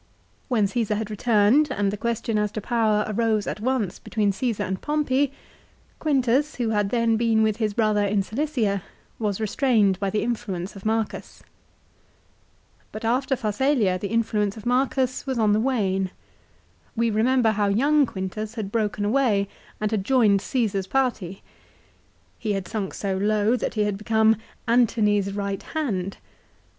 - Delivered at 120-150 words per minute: No, average, 165 wpm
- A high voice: Yes, high, 215 Hz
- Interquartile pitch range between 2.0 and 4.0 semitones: Yes, average, 3.0 semitones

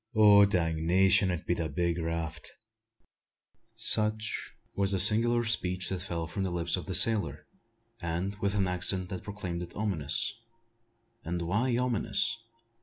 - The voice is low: Yes, very low, 95 Hz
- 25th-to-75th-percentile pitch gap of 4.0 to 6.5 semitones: No, average, 3.3 semitones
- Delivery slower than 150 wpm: Yes, average, 140 wpm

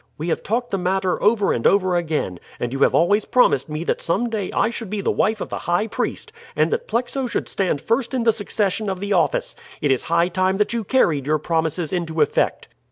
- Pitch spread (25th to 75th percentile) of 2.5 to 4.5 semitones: No, average, 5.1 semitones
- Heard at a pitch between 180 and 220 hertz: Yes, high, 190 Hz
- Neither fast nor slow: No, fast, 230 wpm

